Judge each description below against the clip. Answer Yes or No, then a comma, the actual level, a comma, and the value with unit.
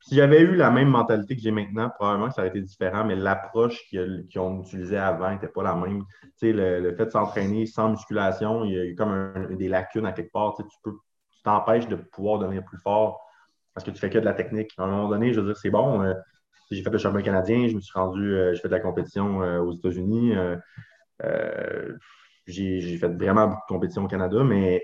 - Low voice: Yes, low, 100 Hz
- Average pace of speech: No, fast, 235 wpm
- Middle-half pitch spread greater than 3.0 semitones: No, average, 2.7 semitones